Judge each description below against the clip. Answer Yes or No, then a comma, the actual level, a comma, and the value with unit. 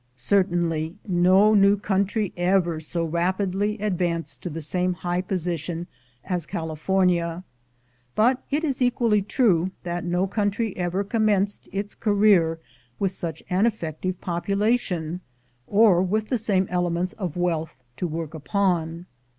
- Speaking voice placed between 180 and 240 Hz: Yes, medium, 185 Hz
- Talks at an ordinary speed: No, slow, 130 wpm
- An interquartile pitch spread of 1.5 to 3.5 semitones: Yes, average, 3.1 semitones